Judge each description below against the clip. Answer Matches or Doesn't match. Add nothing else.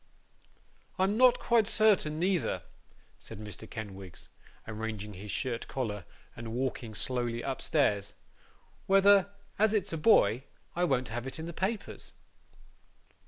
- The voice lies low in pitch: Matches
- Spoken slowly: Matches